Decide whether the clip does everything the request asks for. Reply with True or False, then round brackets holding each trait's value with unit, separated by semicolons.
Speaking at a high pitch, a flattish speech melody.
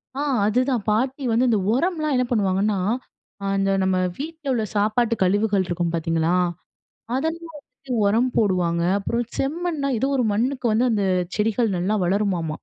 False (220 Hz; 5.2 semitones)